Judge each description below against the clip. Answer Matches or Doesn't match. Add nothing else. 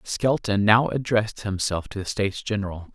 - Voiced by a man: Matches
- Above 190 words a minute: Doesn't match